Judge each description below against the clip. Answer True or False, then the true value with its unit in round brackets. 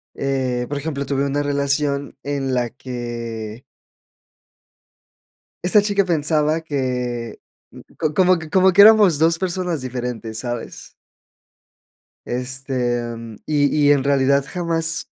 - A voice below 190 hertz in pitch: True (140 Hz)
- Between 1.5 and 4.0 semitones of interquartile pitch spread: False (4.5 semitones)